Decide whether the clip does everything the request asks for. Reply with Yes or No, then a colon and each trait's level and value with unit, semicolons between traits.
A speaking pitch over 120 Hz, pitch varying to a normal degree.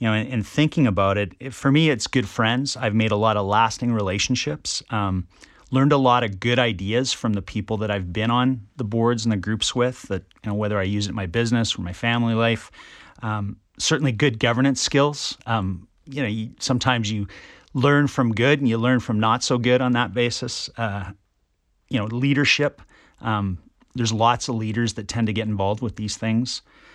No: low, 115 Hz; average, 3.3 semitones